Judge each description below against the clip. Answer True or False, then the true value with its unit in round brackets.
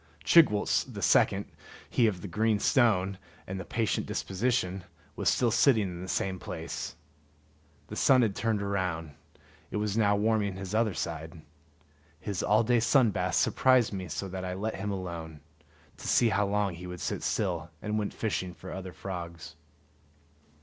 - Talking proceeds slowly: False (170 wpm)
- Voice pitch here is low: True (100 Hz)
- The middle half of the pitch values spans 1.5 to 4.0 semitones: True (3.2 semitones)